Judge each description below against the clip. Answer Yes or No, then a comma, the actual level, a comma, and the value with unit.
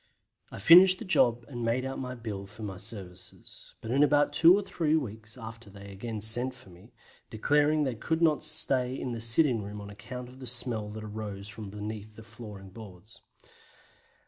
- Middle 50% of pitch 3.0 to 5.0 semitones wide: Yes, average, 3.9 semitones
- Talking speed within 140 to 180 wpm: No, average, 195 wpm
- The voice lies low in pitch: Yes, low, 115 Hz